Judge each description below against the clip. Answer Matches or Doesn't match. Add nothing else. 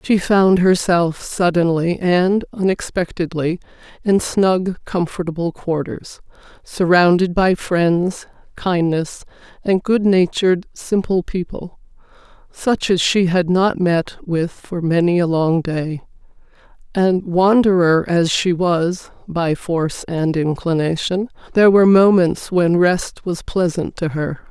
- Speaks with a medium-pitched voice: Matches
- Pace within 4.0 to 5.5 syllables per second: Doesn't match